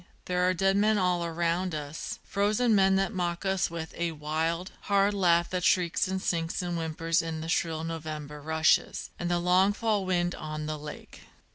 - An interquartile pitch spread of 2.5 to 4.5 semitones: Yes, average, 2.8 semitones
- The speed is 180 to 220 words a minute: Yes, average, 185 wpm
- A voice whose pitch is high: No, medium, 175 Hz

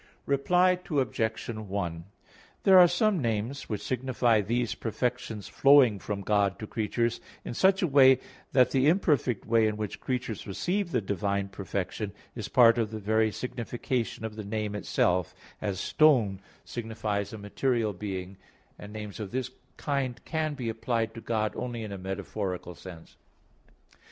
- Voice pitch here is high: No, low, 110 Hz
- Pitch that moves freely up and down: No, average, 4.0 semitones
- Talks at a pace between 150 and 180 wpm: Yes, average, 155 wpm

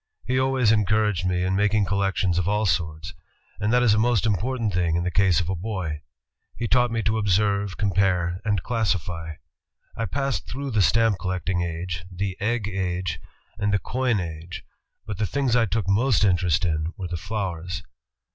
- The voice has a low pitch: Yes, low, 100 Hz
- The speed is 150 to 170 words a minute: No, average, 185 wpm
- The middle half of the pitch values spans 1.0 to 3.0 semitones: No, average, 3.7 semitones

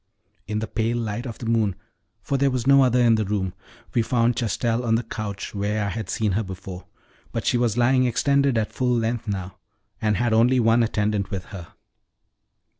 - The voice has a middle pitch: No, low, 115 Hz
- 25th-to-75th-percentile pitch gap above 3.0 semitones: No, average, 2.7 semitones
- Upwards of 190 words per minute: Yes, average, 200 wpm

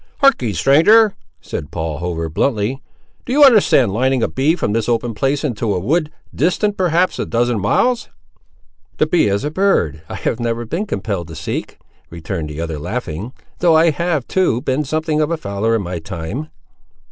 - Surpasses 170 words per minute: Yes, average, 180 wpm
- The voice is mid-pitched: No, low, 125 Hz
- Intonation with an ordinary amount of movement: No, wide, 8.5 semitones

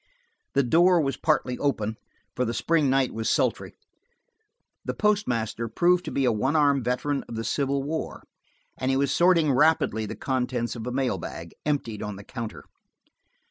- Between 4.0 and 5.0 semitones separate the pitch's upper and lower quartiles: Yes, average, 4.3 semitones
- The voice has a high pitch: No, low, 135 Hz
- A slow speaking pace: No, average, 175 wpm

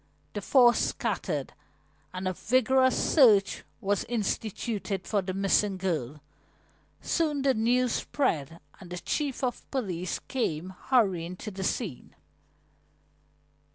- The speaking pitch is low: No, high, 205 Hz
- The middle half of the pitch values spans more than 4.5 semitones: Yes, wide, 5.4 semitones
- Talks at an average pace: No, slow, 120 wpm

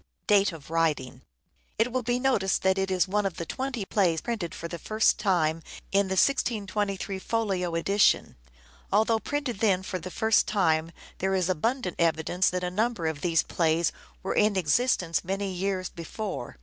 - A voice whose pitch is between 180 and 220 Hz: Yes, high, 190 Hz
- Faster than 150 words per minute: Yes, average, 170 wpm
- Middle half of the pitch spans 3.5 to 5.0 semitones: Yes, average, 3.8 semitones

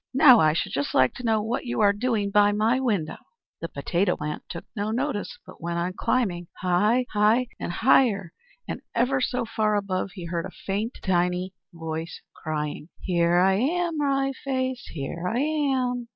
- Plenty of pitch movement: Yes, wide, 6.1 semitones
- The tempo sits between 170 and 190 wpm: Yes, average, 180 wpm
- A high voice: Yes, high, 205 Hz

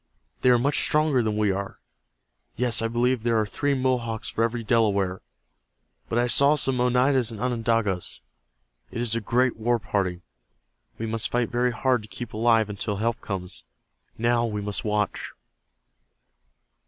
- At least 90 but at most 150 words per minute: No, average, 160 wpm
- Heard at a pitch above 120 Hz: No, low, 115 Hz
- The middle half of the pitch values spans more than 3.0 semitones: No, narrow, 2.6 semitones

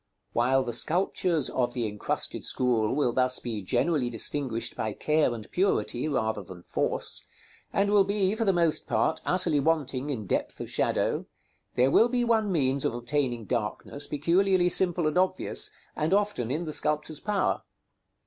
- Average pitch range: No, wide, 6.8 semitones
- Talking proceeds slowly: No, average, 165 wpm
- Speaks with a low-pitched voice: No, medium, 145 Hz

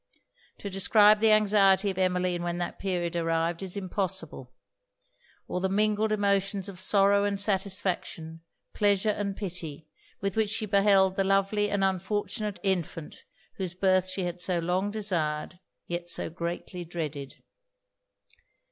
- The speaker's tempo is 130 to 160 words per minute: Yes, average, 140 wpm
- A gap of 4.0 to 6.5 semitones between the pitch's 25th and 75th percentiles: No, narrow, 2.5 semitones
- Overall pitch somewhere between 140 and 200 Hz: Yes, high, 190 Hz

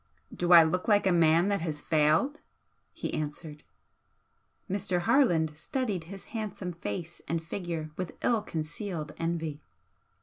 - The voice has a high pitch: No, medium, 170 Hz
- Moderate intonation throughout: Yes, average, 3.6 semitones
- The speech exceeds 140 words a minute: No, slow, 135 wpm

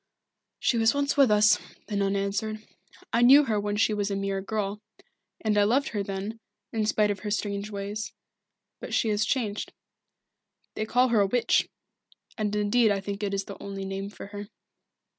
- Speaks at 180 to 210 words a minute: Yes, average, 190 wpm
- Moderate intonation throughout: No, narrow, 1.7 semitones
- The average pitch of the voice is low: No, high, 210 Hz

